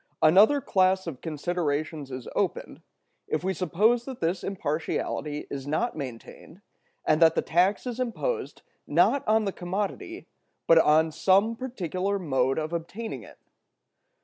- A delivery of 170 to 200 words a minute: No, average, 140 wpm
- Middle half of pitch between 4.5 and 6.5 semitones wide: Yes, average, 5.3 semitones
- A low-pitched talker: No, medium, 175 Hz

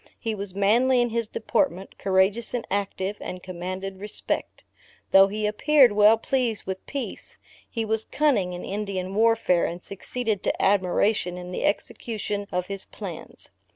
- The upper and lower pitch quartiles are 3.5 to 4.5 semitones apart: No, average, 3.1 semitones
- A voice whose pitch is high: Yes, high, 205 Hz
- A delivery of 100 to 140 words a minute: No, average, 155 wpm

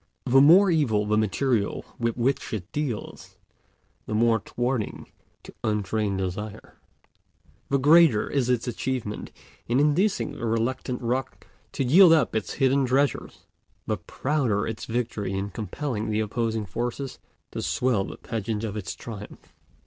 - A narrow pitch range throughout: No, average, 4.1 semitones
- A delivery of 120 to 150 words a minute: Yes, average, 140 wpm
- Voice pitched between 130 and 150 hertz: No, low, 120 Hz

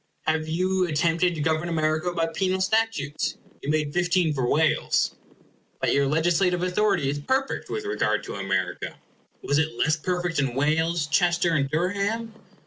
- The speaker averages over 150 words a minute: Yes, average, 160 wpm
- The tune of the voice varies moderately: Yes, average, 3.0 semitones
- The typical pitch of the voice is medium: Yes, medium, 165 Hz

